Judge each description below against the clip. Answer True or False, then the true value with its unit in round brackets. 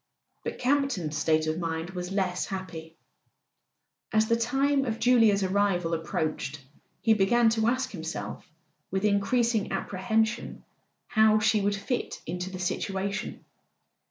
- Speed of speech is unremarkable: False (130 wpm)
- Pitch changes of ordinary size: True (4.0 semitones)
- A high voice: True (200 Hz)